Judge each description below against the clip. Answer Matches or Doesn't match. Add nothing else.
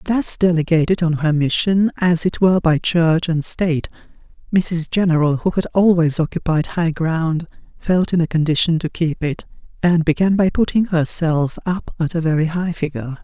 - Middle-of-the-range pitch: Matches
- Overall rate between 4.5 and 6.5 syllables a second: Matches